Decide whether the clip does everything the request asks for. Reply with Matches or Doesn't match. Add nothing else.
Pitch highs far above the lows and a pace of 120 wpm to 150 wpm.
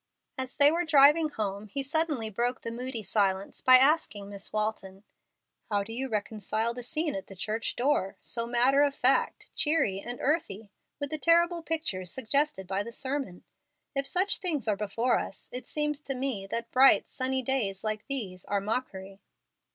Doesn't match